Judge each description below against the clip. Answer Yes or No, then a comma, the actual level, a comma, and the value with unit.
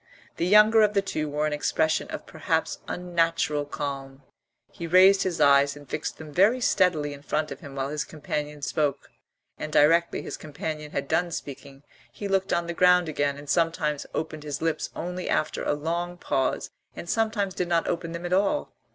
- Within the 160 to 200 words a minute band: Yes, average, 190 wpm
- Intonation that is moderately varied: Yes, average, 3.5 semitones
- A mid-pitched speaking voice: Yes, medium, 160 Hz